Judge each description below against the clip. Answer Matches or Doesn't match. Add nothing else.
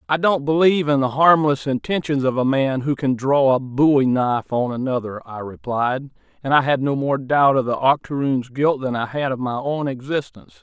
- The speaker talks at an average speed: Doesn't match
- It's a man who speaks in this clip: Matches